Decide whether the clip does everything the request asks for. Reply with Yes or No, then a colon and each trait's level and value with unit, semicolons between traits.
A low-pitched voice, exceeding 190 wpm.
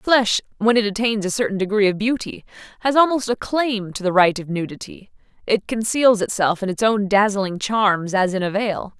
No: high, 210 Hz; average, 200 wpm